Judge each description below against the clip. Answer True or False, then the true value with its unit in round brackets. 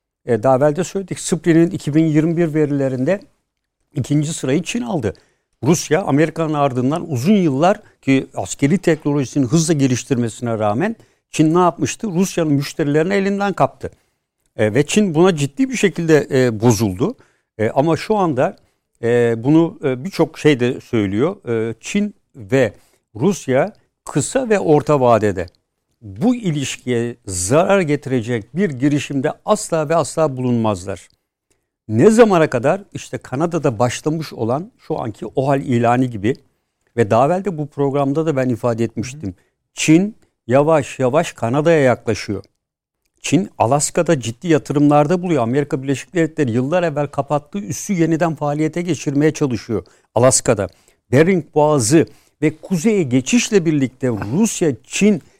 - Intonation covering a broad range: False (4.8 semitones)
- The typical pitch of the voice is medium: True (145 Hz)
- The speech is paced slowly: False (120 wpm)